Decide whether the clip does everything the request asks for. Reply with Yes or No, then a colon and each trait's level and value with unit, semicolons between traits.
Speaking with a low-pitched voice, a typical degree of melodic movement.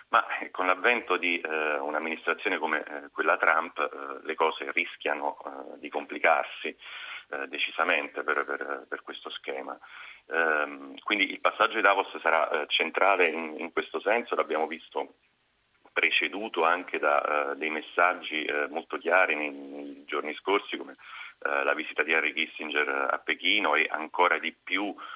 Yes: very low, 80 Hz; average, 4.2 semitones